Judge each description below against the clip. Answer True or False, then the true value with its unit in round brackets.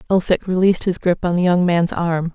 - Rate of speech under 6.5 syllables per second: True (5.6 syllables/s)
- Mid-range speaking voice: True (175 Hz)